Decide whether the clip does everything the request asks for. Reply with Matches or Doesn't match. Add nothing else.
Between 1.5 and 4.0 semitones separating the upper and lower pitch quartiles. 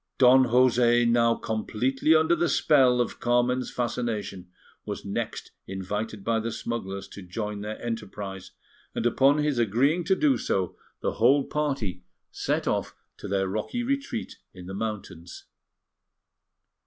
Doesn't match